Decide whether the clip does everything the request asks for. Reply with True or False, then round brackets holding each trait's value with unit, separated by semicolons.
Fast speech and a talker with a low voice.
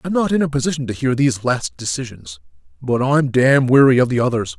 True (220 wpm; 125 Hz)